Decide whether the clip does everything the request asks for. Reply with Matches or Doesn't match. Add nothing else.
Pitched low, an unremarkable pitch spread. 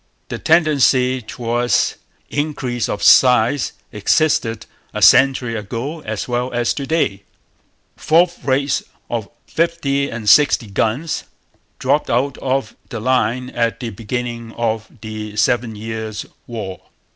Matches